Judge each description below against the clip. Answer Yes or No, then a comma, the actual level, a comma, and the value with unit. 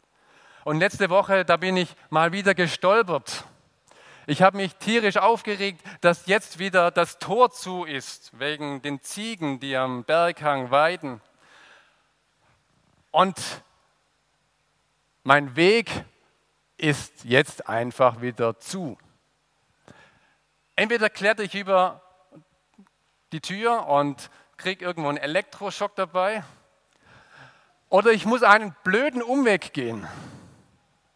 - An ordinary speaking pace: No, slow, 105 wpm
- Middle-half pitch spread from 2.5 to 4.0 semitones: No, wide, 5.6 semitones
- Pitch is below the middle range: No, medium, 180 Hz